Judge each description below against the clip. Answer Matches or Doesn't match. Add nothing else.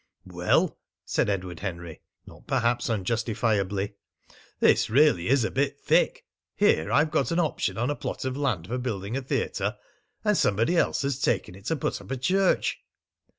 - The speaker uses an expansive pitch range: Matches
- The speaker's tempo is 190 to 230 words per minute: Doesn't match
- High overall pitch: Doesn't match